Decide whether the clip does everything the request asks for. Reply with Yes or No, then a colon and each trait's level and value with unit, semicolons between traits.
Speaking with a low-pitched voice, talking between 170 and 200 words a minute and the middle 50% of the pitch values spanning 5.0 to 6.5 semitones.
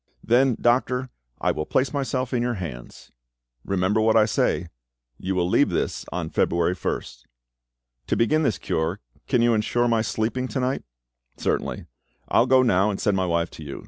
Yes: low, 110 Hz; average, 180 wpm; wide, 5.5 semitones